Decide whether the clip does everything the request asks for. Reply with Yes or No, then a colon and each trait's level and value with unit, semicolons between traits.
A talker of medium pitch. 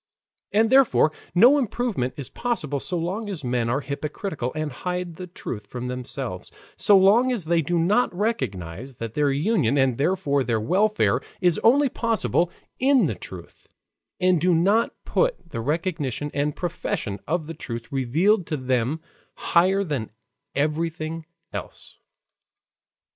Yes: medium, 165 Hz